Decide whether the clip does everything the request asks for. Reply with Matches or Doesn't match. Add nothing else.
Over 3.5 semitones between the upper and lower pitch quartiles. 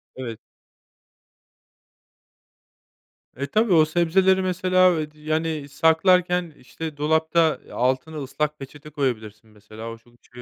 Matches